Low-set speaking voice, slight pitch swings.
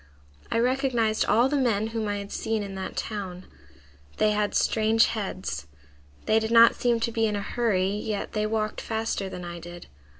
No: high, 215 Hz; narrow, 2.3 semitones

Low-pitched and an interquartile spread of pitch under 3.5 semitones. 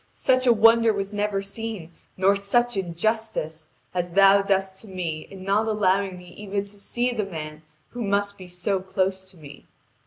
No: high, 195 Hz; narrow, 2.4 semitones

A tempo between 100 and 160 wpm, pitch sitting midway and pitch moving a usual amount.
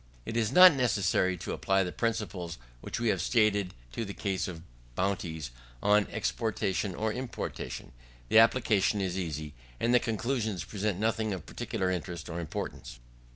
No: average, 155 wpm; low, 100 Hz; average, 3.8 semitones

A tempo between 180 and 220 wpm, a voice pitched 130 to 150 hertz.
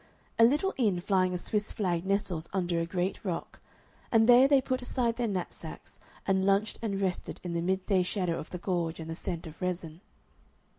No: average, 200 wpm; high, 190 Hz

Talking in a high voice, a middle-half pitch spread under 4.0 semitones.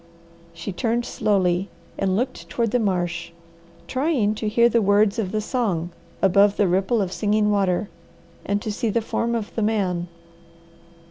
Yes: high, 205 Hz; average, 3.2 semitones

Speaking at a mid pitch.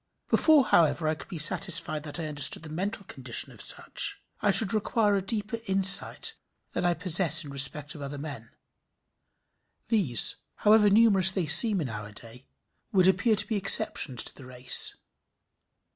Yes: medium, 170 Hz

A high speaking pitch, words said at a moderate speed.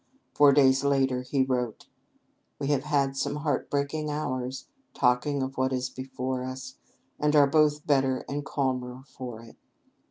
No: low, 135 Hz; average, 155 wpm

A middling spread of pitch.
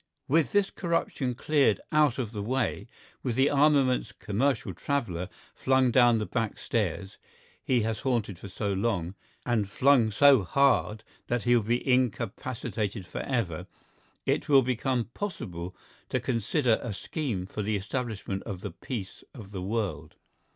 Yes: average, 4.5 semitones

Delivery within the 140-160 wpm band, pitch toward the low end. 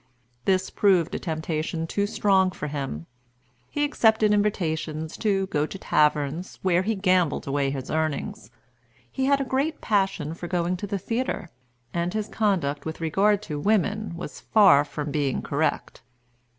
No: average, 155 wpm; medium, 180 Hz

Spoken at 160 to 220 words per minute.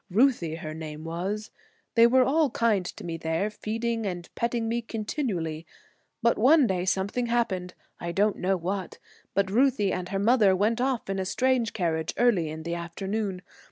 Yes: average, 175 wpm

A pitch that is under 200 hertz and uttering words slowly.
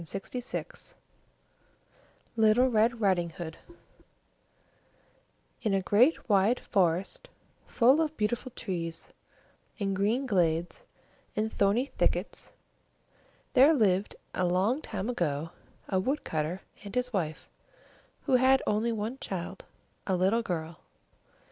No: high, 205 Hz; slow, 110 wpm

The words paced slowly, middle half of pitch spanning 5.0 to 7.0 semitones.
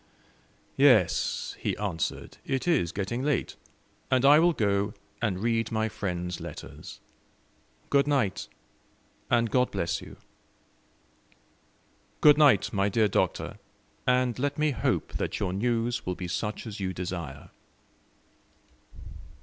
Yes: slow, 125 wpm; average, 5.3 semitones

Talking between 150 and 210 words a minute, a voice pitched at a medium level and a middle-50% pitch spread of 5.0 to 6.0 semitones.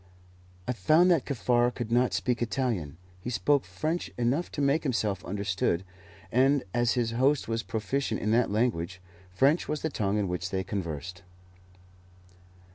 No: average, 155 wpm; low, 120 Hz; wide, 5.6 semitones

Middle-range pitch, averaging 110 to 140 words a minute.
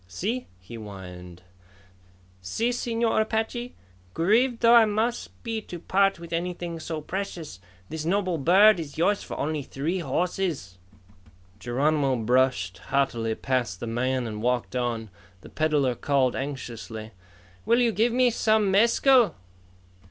Yes: medium, 155 Hz; slow, 135 wpm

